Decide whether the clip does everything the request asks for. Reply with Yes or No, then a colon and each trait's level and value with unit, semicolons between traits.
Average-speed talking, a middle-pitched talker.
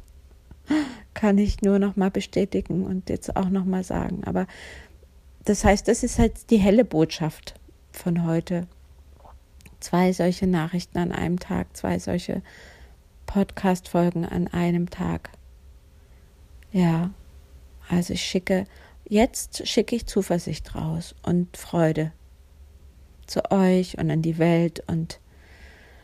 No: slow, 120 wpm; medium, 165 Hz